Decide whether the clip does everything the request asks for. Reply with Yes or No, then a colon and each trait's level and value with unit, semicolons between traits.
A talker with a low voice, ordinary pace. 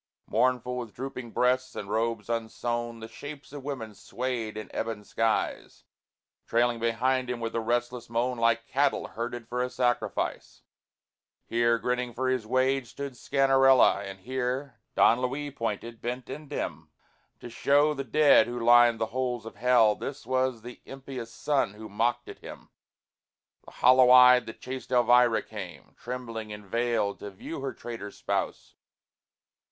Yes: low, 120 Hz; average, 155 wpm